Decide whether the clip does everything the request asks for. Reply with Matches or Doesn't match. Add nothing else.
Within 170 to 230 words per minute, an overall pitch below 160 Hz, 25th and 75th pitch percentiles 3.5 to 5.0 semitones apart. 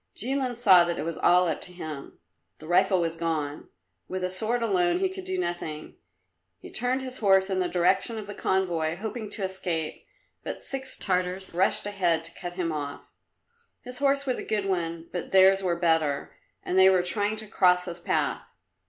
Doesn't match